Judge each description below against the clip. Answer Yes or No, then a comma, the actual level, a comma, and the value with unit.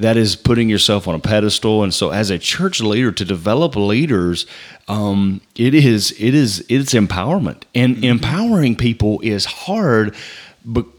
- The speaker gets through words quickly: No, average, 160 wpm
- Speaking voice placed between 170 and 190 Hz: No, low, 110 Hz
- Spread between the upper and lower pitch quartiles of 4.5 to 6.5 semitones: No, average, 3.3 semitones